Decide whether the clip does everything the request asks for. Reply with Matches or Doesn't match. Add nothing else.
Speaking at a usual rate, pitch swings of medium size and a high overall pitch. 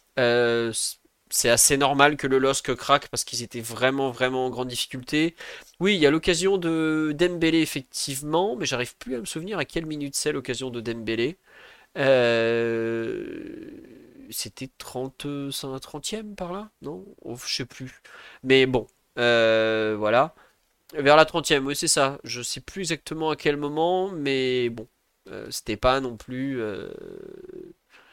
Doesn't match